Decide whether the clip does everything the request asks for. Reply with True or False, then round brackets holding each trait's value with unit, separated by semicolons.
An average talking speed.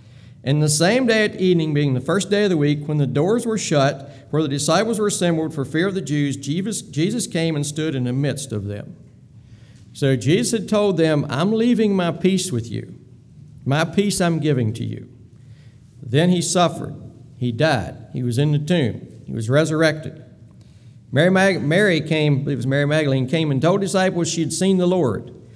True (195 wpm)